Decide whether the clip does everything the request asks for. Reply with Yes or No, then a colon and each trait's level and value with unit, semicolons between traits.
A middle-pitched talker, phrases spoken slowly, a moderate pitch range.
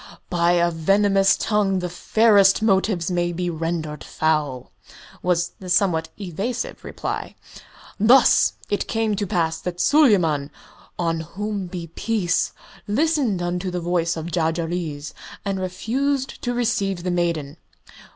Yes: medium, 180 Hz; slow, 130 wpm; average, 3.6 semitones